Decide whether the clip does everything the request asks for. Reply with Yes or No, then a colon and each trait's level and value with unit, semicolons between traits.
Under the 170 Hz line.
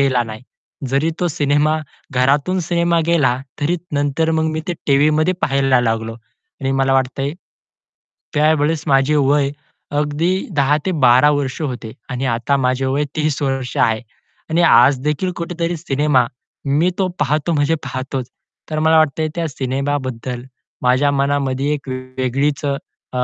Yes: medium, 140 Hz